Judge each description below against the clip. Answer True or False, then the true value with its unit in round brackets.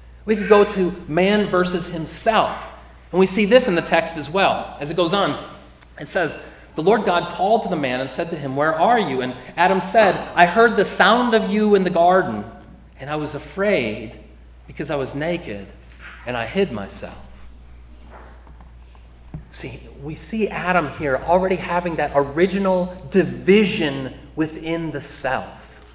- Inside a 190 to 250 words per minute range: False (170 wpm)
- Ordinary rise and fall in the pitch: False (6.0 semitones)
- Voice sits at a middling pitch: True (170 Hz)